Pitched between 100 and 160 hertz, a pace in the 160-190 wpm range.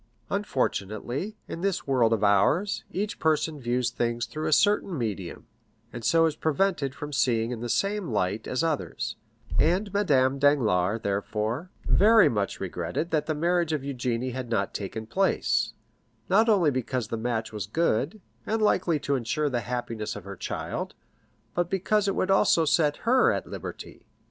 Yes: medium, 140 Hz; average, 165 wpm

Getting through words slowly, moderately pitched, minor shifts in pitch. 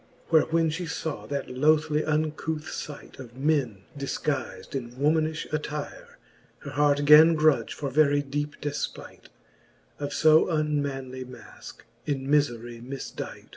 Yes: slow, 130 wpm; medium, 145 Hz; narrow, 2.2 semitones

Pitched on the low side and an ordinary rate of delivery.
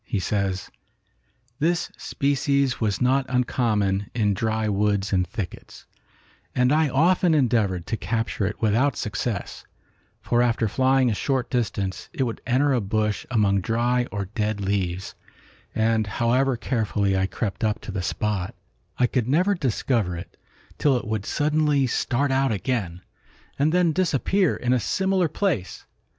Yes: low, 115 Hz; average, 150 wpm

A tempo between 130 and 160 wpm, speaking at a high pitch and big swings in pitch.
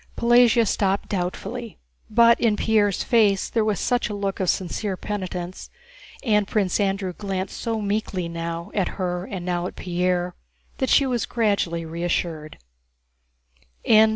No: average, 140 wpm; high, 195 Hz; average, 3.5 semitones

